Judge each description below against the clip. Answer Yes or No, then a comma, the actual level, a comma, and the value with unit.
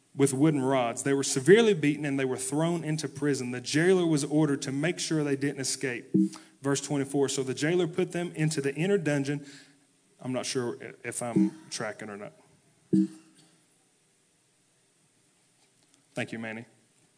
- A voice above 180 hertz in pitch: No, medium, 140 Hz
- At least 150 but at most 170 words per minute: Yes, average, 155 wpm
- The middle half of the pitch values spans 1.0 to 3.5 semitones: Yes, narrow, 2.6 semitones